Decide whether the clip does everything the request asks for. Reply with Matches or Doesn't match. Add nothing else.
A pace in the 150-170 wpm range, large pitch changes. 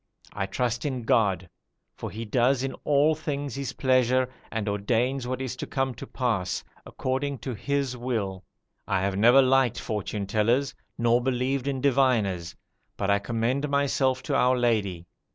Doesn't match